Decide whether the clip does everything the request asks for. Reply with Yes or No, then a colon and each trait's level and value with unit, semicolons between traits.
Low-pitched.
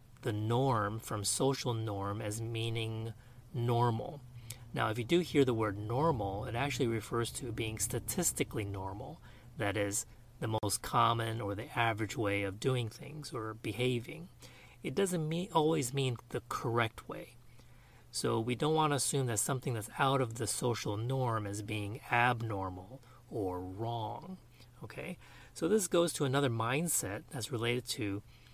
Yes: low, 120 Hz